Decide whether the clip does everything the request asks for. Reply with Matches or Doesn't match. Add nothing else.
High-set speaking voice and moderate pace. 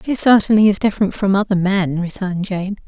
Matches